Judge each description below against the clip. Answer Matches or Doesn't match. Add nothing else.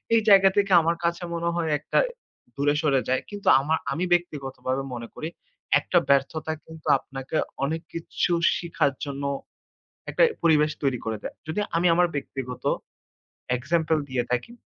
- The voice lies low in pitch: Doesn't match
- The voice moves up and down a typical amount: Matches